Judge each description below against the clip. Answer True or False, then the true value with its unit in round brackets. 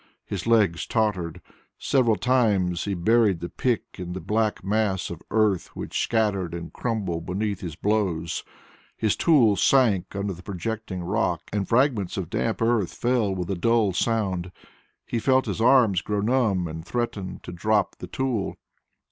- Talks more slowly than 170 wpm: True (160 wpm)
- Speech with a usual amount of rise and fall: True (4.0 semitones)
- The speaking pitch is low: True (105 Hz)